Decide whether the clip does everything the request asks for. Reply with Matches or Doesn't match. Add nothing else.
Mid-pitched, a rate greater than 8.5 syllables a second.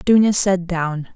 Doesn't match